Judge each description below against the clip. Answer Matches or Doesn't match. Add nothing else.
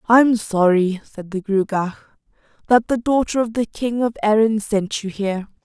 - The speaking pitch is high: Matches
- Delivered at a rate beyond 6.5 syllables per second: Doesn't match